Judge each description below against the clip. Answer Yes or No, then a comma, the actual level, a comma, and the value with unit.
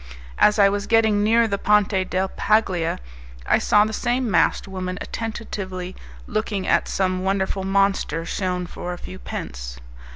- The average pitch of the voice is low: No, high, 195 Hz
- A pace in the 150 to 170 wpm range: Yes, average, 155 wpm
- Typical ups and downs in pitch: No, narrow, 2.3 semitones